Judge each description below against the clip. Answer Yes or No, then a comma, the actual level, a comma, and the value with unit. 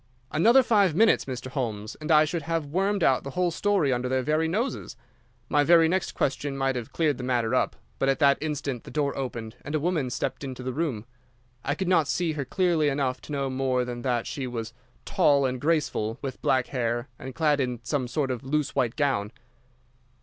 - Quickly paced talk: Yes, fast, 215 wpm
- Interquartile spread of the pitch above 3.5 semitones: Yes, average, 3.9 semitones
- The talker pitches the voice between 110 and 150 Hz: Yes, medium, 140 Hz